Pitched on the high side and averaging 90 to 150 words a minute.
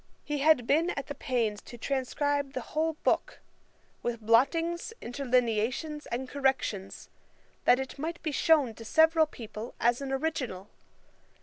Yes: very high, 270 Hz; average, 140 wpm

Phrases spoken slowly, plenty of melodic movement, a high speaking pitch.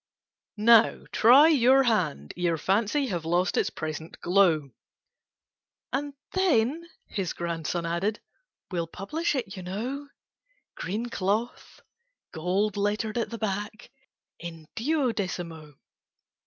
Yes: slow, 105 wpm; wide, 5.9 semitones; high, 205 Hz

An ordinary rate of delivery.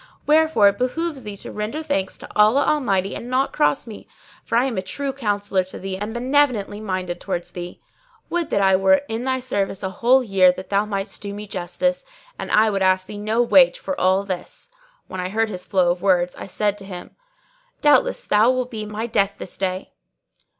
No: fast, 210 wpm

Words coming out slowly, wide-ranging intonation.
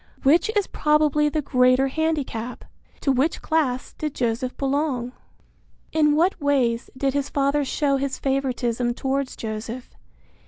No: slow, 130 wpm; average, 3.0 semitones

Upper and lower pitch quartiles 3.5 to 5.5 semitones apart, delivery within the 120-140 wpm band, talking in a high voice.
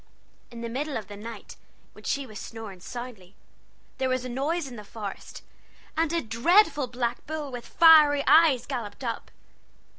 No: average, 4.4 semitones; average, 170 wpm; very high, 250 Hz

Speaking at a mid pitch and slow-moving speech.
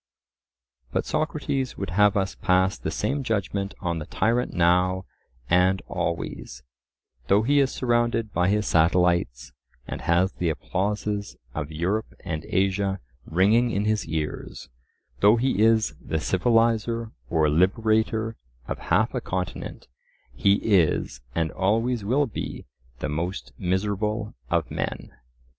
No: low, 100 Hz; slow, 130 wpm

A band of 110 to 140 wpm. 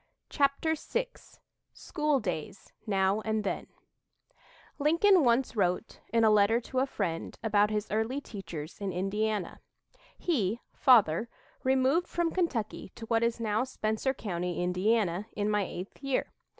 Yes: slow, 135 wpm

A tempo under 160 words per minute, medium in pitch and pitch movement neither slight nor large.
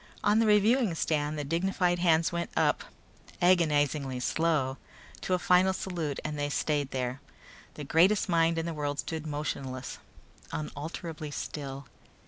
Yes: average, 140 wpm; medium, 160 Hz; average, 3.3 semitones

